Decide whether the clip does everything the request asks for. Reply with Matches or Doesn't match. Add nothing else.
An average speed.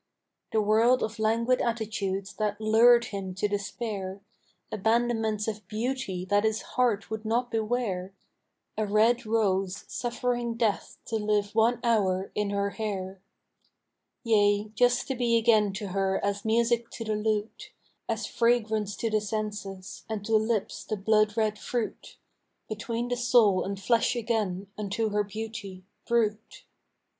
Matches